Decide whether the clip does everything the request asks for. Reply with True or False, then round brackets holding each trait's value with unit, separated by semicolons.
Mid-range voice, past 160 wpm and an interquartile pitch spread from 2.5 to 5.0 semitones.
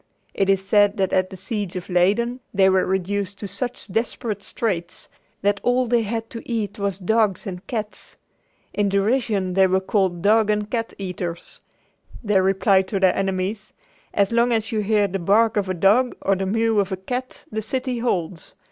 False (200 Hz; 190 wpm; 2.9 semitones)